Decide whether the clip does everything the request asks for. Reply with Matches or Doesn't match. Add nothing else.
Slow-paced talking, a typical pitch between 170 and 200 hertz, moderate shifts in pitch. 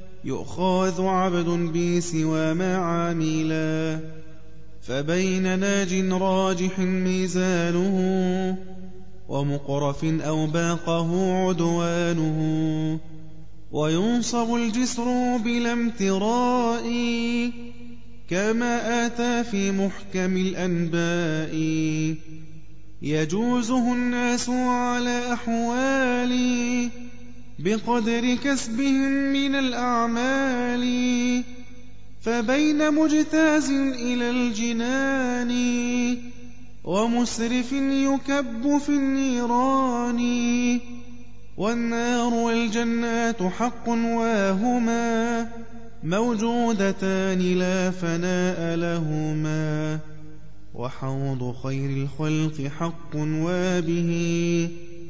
Doesn't match